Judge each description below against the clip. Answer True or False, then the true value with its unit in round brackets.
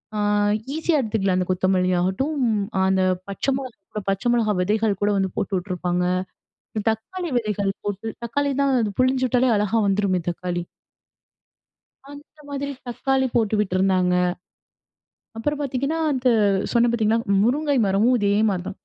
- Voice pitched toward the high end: True (215 Hz)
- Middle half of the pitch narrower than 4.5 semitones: False (5.2 semitones)